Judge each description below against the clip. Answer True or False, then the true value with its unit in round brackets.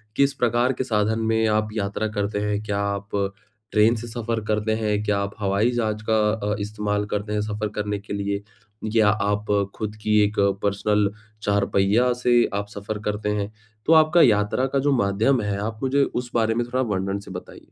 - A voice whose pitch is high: False (105 Hz)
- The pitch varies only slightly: True (1.7 semitones)